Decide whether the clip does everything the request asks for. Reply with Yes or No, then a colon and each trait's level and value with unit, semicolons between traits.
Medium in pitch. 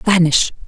Yes: medium, 175 Hz